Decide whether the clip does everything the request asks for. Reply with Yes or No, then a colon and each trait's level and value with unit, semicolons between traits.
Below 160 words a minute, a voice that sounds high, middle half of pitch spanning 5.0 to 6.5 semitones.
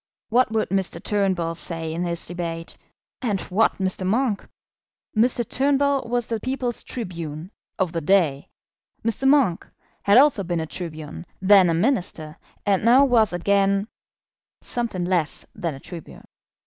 Yes: average, 145 wpm; high, 195 Hz; wide, 5.6 semitones